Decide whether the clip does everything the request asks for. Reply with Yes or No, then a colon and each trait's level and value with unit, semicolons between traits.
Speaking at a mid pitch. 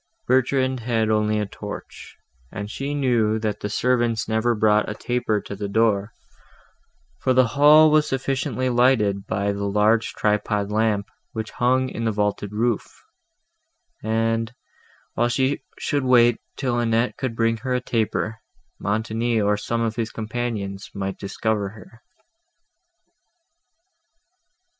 No: low, 115 Hz